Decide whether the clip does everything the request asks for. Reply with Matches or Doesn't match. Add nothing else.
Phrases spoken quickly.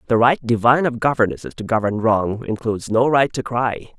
Doesn't match